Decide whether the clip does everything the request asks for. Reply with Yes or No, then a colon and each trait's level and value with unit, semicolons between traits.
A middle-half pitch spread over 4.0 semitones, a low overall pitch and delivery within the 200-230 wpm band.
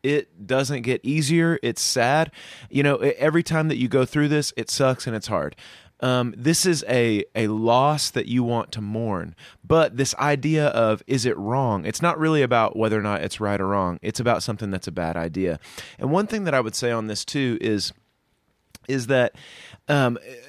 Yes: average, 5.1 semitones; low, 125 Hz; fast, 205 wpm